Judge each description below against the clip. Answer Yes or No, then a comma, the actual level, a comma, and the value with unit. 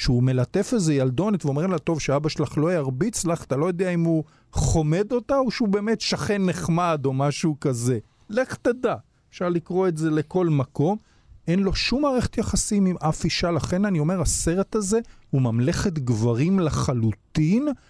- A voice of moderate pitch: Yes, medium, 170 Hz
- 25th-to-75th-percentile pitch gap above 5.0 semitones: Yes, wide, 5.4 semitones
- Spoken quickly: Yes, fast, 175 wpm